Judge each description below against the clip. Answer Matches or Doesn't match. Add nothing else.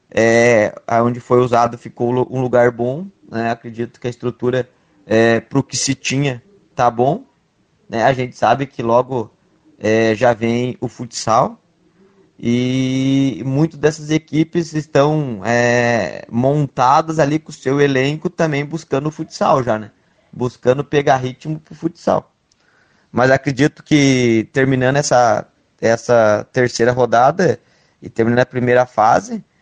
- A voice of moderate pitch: Doesn't match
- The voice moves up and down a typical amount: Matches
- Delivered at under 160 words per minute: Matches